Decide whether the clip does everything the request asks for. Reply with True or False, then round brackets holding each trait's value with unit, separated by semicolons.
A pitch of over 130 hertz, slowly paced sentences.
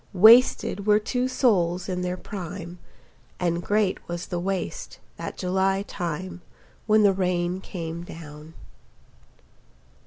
True (185 Hz; 120 wpm)